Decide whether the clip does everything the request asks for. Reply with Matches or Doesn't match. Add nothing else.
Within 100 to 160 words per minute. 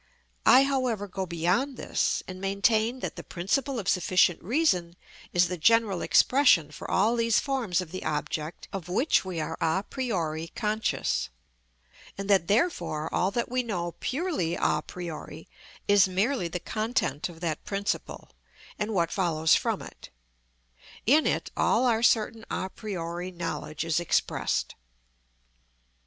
Matches